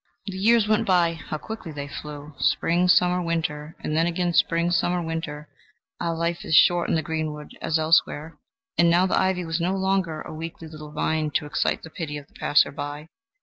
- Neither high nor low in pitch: Yes, medium, 165 Hz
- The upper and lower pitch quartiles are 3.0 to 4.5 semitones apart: No, narrow, 2.5 semitones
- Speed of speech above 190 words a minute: Yes, average, 200 wpm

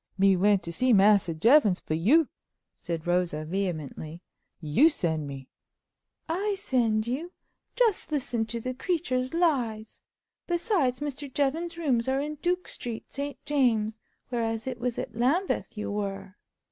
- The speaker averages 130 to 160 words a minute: Yes, average, 145 wpm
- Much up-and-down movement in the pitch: Yes, wide, 7.0 semitones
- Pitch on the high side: Yes, high, 240 Hz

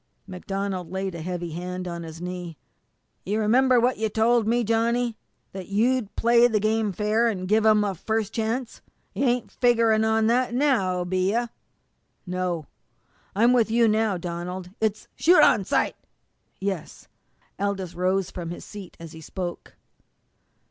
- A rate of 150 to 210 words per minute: Yes, average, 160 wpm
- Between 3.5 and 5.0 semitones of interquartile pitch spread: Yes, average, 4.0 semitones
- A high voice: Yes, high, 210 Hz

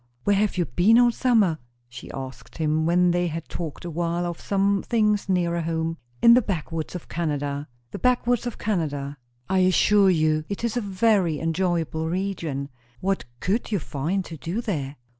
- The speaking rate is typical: Yes, average, 175 wpm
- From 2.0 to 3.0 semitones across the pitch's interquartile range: No, average, 4.1 semitones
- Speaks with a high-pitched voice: No, medium, 175 Hz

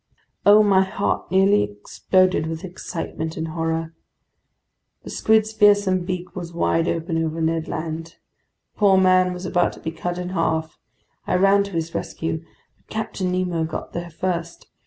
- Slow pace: No, average, 160 wpm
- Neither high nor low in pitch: Yes, medium, 175 Hz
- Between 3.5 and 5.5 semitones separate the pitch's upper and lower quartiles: No, narrow, 2.5 semitones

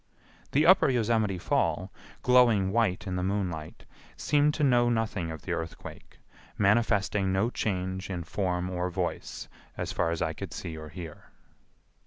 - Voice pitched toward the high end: No, very low, 95 Hz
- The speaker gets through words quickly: No, average, 155 wpm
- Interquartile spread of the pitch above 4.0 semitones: Yes, average, 4.7 semitones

